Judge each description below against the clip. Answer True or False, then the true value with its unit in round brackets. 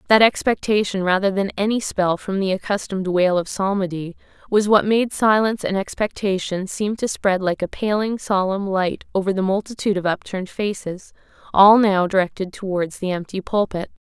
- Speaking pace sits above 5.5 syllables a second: False (5.3 syllables/s)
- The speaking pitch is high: True (195 Hz)